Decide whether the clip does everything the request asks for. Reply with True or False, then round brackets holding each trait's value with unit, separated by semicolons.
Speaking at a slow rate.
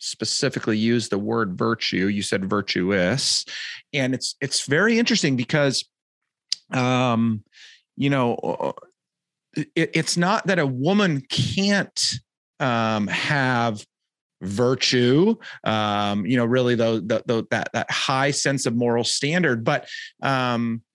True (115 wpm)